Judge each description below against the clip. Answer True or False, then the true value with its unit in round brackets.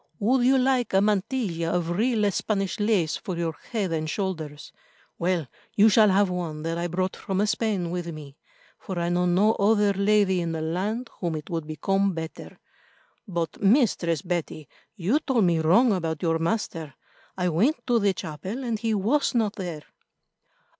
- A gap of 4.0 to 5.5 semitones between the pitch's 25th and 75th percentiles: True (4.3 semitones)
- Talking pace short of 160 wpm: False (175 wpm)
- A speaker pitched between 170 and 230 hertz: True (190 Hz)